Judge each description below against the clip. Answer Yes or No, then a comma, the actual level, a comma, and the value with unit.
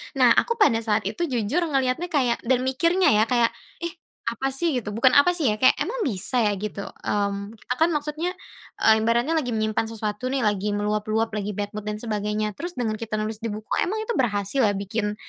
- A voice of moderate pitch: No, high, 230 Hz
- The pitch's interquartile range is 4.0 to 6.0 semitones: Yes, average, 4.4 semitones